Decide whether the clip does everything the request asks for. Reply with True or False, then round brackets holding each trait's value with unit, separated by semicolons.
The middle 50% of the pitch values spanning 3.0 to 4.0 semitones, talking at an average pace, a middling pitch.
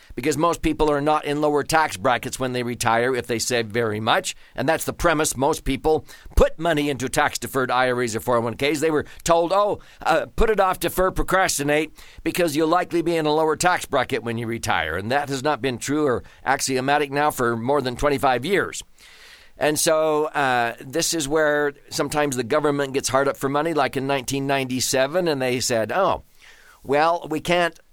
True (3.5 semitones; 195 wpm; 145 Hz)